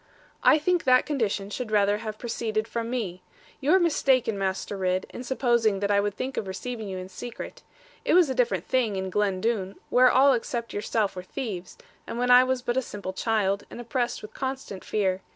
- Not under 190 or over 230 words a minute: Yes, fast, 205 wpm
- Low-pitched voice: No, high, 225 Hz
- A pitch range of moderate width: Yes, average, 4.2 semitones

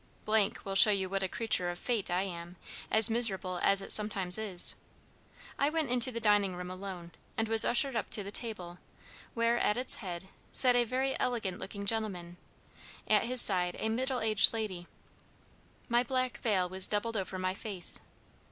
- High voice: Yes, high, 210 Hz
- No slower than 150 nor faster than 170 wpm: No, average, 180 wpm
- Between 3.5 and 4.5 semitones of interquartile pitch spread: Yes, average, 3.9 semitones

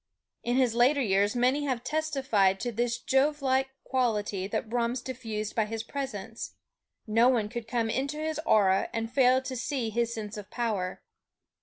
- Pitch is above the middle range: Yes, high, 235 Hz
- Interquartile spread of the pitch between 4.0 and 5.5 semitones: No, average, 3.3 semitones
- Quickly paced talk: No, average, 165 wpm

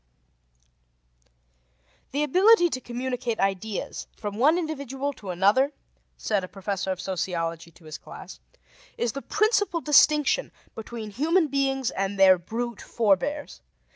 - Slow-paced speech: Yes, slow, 130 wpm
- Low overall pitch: No, high, 240 Hz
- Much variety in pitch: Yes, wide, 6.9 semitones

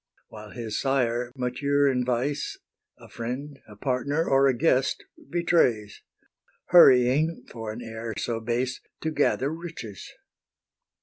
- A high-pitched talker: No, low, 125 Hz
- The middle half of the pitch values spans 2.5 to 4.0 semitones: Yes, average, 3.5 semitones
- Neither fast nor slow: No, slow, 125 wpm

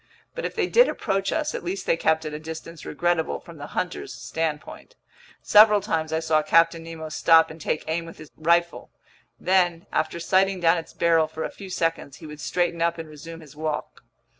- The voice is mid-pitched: Yes, medium, 165 Hz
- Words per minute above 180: Yes, fast, 205 wpm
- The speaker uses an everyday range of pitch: No, narrow, 1.8 semitones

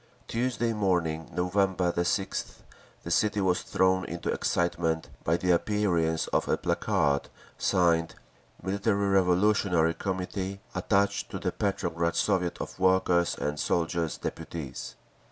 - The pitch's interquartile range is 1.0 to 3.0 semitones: Yes, narrow, 2.6 semitones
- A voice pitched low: Yes, very low, 90 Hz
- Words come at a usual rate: No, slow, 120 wpm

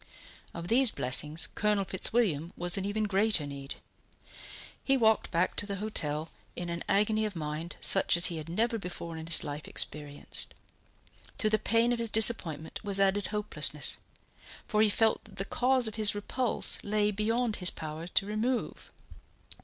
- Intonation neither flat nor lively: Yes, average, 4.5 semitones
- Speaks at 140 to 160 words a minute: No, average, 170 wpm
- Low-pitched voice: No, high, 200 Hz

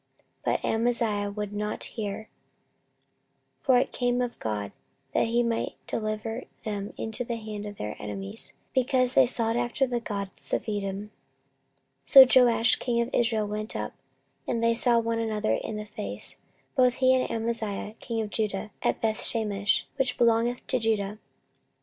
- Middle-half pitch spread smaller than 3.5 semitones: Yes, narrow, 2.5 semitones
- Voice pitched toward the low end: No, high, 225 Hz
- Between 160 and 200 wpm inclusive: Yes, average, 165 wpm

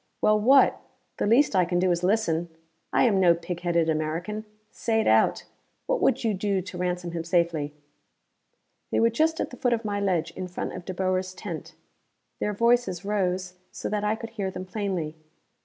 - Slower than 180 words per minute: No, average, 195 wpm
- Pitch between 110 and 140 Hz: No, medium, 185 Hz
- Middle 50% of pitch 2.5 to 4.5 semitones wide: Yes, average, 3.5 semitones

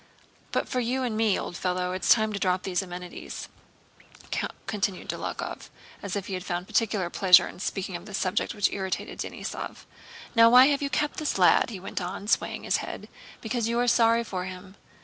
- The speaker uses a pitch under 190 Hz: No, high, 200 Hz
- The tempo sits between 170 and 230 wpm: Yes, average, 190 wpm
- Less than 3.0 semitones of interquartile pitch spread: No, average, 4.0 semitones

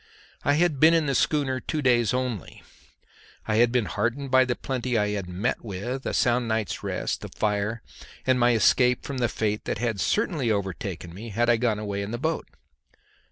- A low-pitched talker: Yes, low, 120 Hz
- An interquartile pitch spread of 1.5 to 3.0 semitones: No, average, 3.7 semitones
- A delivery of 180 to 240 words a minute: Yes, average, 200 wpm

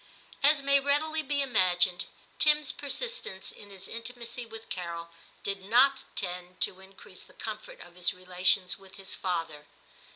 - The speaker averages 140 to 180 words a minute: Yes, average, 155 wpm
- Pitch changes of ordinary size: No, wide, 7.2 semitones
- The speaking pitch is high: Yes, high, 200 Hz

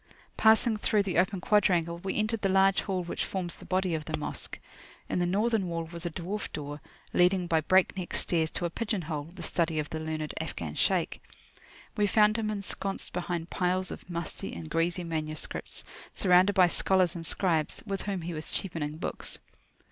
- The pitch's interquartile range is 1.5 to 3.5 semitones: Yes, average, 3.0 semitones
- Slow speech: No, average, 185 wpm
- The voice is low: No, medium, 180 Hz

